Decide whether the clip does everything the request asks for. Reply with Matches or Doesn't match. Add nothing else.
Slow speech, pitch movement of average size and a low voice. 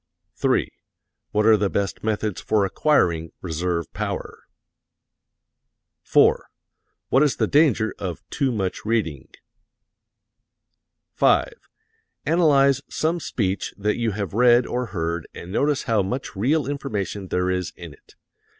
Doesn't match